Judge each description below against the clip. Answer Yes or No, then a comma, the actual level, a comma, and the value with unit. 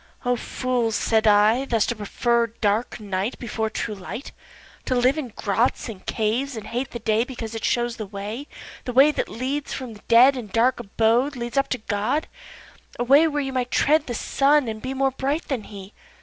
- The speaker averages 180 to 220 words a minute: Yes, average, 200 wpm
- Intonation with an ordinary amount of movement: Yes, average, 3.4 semitones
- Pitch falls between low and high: No, high, 240 Hz